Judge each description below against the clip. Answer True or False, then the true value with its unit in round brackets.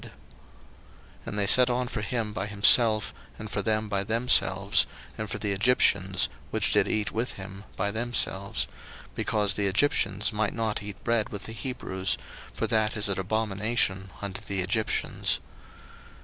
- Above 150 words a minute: True (160 wpm)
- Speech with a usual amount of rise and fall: False (2.1 semitones)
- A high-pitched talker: False (105 Hz)